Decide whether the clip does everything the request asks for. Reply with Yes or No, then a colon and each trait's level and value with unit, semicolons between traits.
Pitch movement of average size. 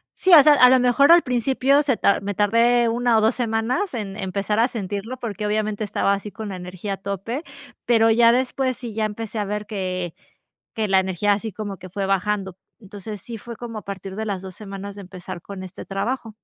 Yes: average, 3.3 semitones